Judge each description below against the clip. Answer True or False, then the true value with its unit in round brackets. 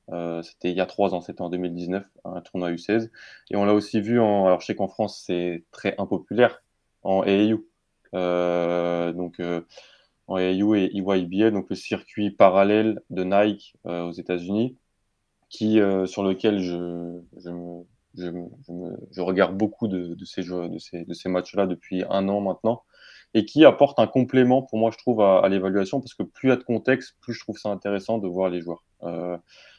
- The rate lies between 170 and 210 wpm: True (200 wpm)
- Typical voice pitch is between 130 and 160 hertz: False (95 Hz)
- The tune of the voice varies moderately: True (3.5 semitones)